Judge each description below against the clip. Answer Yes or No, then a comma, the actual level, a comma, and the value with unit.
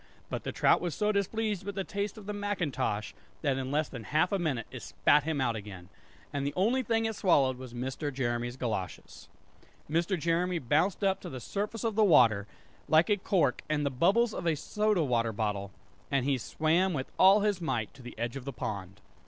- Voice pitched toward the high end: No, medium, 155 Hz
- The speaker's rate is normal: No, fast, 215 wpm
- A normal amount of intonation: No, wide, 8.0 semitones